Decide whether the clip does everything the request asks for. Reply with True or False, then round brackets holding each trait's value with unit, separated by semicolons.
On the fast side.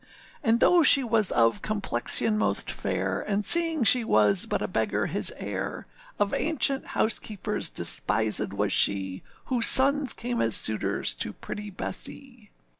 False (145 wpm)